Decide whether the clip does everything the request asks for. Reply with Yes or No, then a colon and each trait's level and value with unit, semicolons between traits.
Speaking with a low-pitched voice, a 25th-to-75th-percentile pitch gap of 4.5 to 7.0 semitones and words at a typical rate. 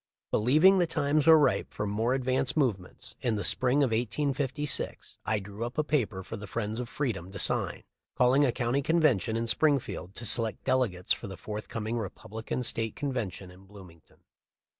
Yes: low, 120 Hz; average, 4.9 semitones; average, 175 wpm